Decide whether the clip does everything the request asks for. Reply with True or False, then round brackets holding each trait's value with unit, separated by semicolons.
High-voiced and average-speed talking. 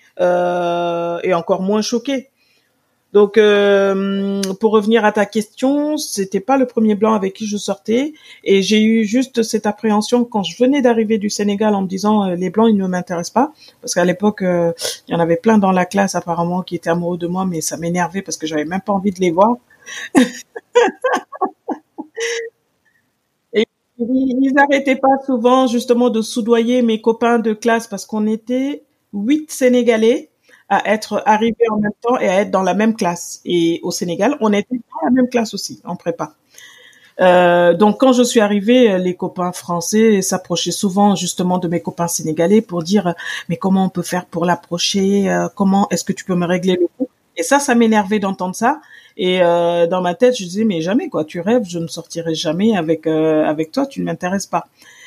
True (205 Hz; 195 wpm)